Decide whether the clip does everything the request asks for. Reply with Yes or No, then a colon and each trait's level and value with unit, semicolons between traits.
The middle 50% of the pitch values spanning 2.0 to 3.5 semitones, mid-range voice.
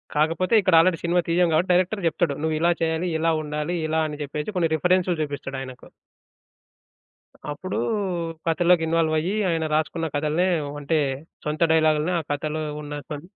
Yes: narrow, 2.5 semitones; medium, 160 Hz